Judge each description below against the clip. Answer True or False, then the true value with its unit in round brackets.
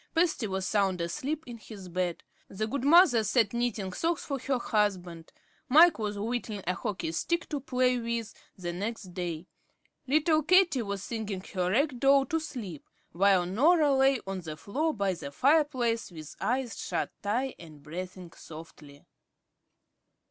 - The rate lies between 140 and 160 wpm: True (155 wpm)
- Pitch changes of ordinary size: False (6.8 semitones)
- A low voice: False (220 Hz)